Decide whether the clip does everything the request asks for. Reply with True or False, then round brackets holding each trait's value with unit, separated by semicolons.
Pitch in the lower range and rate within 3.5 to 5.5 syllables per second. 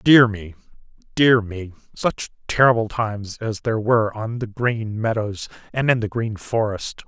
True (110 Hz; 4.5 syllables/s)